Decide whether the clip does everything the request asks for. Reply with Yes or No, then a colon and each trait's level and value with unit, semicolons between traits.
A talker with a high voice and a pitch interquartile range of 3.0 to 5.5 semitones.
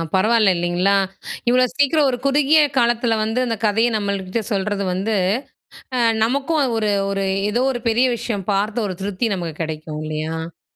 Yes: high, 210 Hz; average, 4.2 semitones